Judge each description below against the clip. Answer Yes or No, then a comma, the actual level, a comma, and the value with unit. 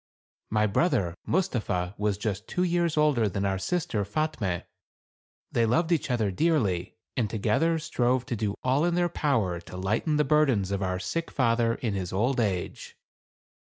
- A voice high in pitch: No, low, 115 Hz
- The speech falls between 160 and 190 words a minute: Yes, average, 165 wpm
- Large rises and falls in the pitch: Yes, wide, 7.4 semitones